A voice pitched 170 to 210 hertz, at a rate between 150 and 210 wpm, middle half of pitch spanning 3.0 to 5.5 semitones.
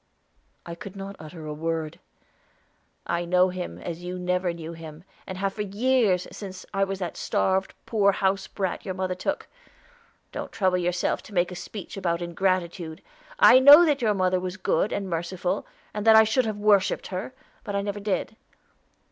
No: medium, 185 Hz; average, 180 wpm; narrow, 2.5 semitones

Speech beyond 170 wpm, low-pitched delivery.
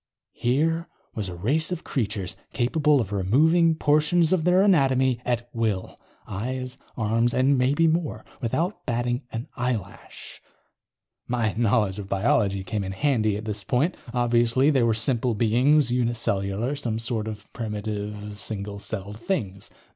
No: average, 145 wpm; low, 120 Hz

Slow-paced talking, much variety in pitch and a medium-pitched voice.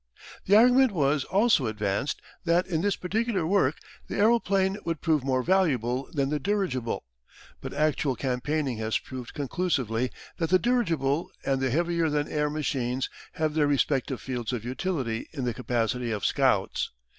No: average, 155 wpm; wide, 6.0 semitones; medium, 145 Hz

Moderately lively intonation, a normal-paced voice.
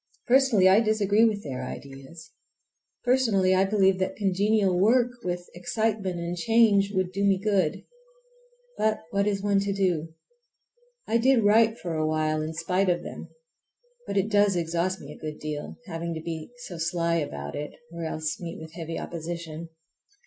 Yes: average, 3.9 semitones; average, 165 wpm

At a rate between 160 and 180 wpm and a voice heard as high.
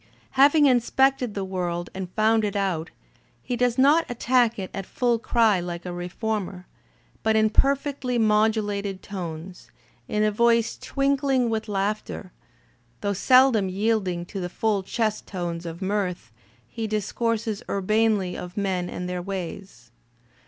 No: average, 140 wpm; high, 210 Hz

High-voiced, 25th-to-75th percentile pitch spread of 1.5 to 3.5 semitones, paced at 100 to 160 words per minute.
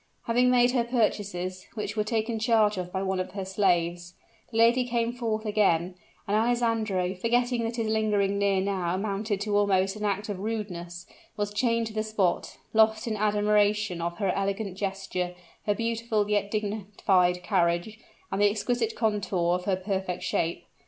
No: high, 205 Hz; average, 2.8 semitones; average, 170 wpm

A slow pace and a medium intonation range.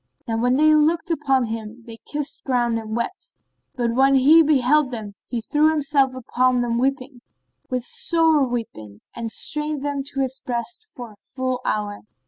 No: average, 170 wpm; average, 4.0 semitones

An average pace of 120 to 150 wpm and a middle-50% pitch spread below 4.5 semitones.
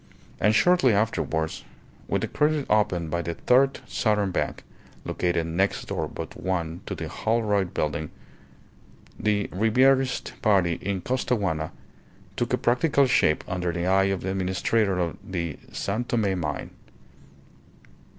No: slow, 135 wpm; average, 4.9 semitones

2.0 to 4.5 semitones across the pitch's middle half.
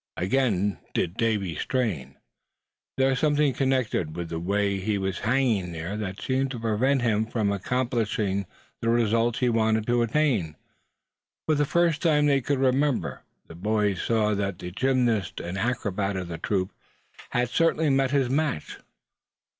No: average, 5.1 semitones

